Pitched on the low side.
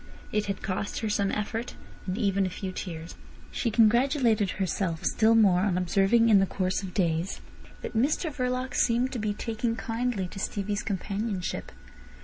No: high, 210 Hz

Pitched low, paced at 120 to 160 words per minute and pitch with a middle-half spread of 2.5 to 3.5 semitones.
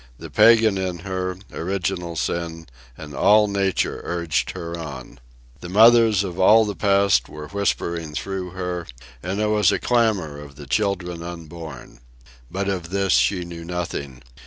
Yes: very low, 90 Hz; average, 155 wpm; average, 3.0 semitones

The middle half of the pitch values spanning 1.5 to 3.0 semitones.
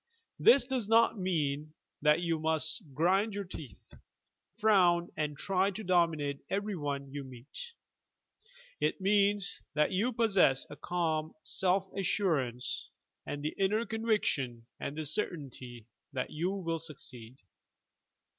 No: wide, 5.4 semitones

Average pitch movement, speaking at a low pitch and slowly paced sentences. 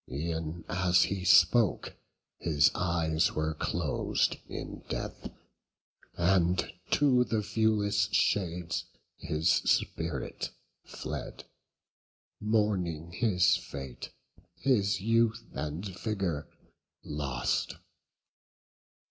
Yes: average, 4.8 semitones; very low, 90 Hz; slow, 80 wpm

